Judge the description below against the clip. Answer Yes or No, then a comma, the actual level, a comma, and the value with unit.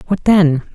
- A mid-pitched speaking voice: Yes, medium, 175 Hz